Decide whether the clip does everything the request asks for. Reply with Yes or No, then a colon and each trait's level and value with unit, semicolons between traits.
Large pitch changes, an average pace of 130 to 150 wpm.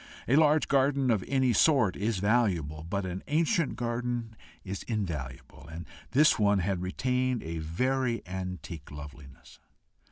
Yes: wide, 7.0 semitones; slow, 135 wpm